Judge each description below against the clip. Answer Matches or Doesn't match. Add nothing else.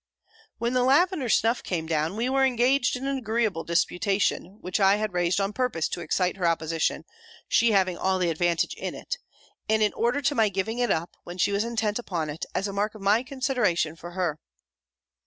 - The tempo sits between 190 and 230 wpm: Matches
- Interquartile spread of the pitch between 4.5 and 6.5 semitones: Matches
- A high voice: Matches